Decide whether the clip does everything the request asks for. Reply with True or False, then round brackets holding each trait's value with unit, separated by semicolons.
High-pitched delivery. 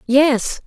True (265 Hz)